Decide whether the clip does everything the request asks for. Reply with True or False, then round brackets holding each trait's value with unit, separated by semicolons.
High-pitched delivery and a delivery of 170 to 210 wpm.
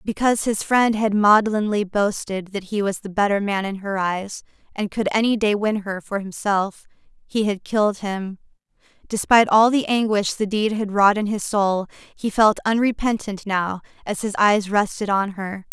True (205 Hz; 185 wpm)